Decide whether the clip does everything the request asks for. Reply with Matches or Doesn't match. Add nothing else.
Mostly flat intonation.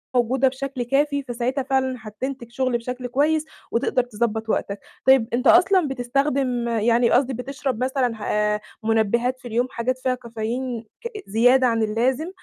Matches